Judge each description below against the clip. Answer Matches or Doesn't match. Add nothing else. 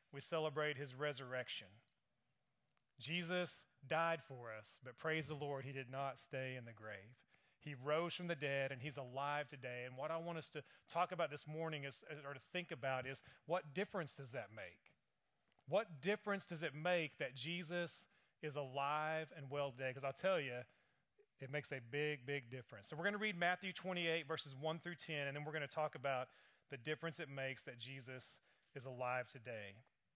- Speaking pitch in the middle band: Matches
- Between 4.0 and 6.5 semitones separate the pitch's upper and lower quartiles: Doesn't match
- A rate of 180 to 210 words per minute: Matches